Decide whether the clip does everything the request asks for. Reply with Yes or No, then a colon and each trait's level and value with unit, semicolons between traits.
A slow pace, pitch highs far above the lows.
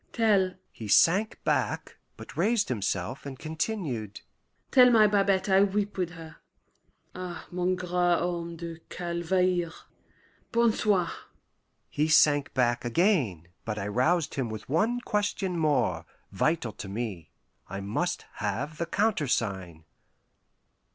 Yes: slow, 125 wpm; wide, 8.1 semitones